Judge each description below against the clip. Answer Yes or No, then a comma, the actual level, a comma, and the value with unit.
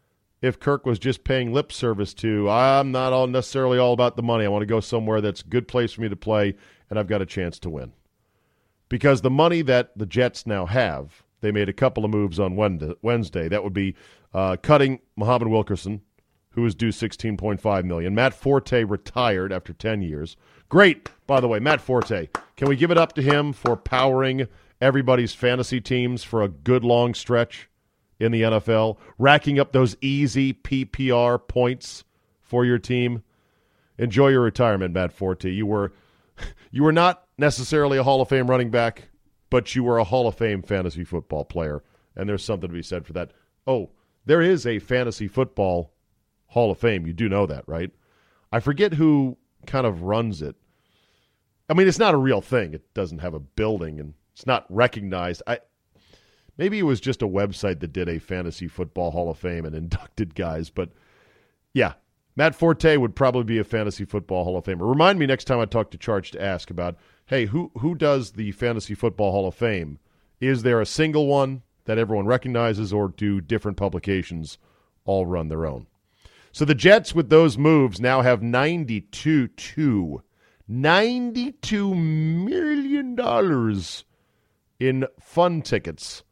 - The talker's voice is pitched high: No, low, 115 Hz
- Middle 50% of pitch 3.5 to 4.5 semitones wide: No, average, 4.9 semitones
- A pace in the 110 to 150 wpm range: No, average, 185 wpm